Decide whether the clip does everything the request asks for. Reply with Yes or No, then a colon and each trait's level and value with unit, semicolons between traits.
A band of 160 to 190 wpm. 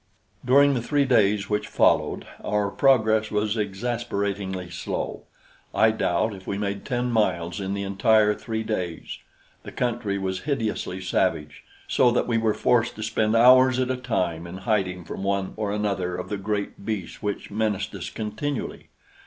Yes: average, 165 wpm